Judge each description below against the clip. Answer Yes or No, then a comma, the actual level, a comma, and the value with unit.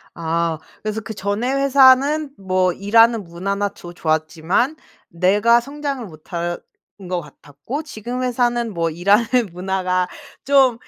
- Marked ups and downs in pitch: Yes, wide, 6.0 semitones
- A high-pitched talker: Yes, high, 205 Hz